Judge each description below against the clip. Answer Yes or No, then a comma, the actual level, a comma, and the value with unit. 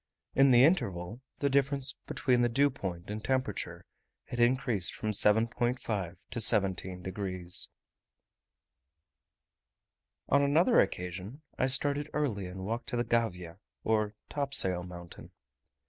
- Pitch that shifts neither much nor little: No, wide, 6.2 semitones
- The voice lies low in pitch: Yes, low, 115 Hz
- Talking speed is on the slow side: Yes, slow, 120 wpm